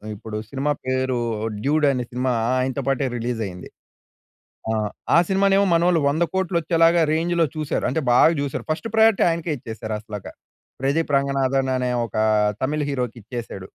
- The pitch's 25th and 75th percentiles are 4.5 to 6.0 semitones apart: Yes, average, 5.0 semitones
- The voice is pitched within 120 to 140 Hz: Yes, low, 135 Hz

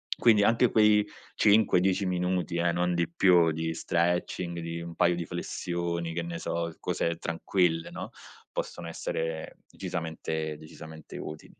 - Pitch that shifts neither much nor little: No, narrow, 1.5 semitones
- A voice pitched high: No, very low, 85 Hz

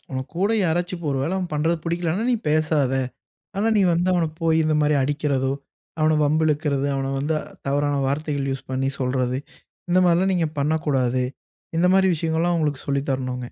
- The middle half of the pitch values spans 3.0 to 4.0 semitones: Yes, average, 3.6 semitones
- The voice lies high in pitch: No, medium, 155 Hz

